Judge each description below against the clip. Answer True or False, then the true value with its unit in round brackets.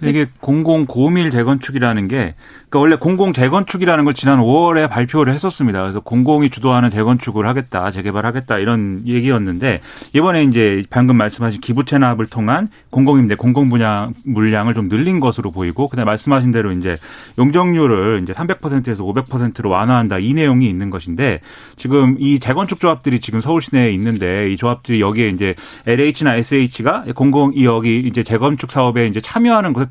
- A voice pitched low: True (125 Hz)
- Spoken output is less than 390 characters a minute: False (400 characters per minute)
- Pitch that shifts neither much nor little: True (4.2 semitones)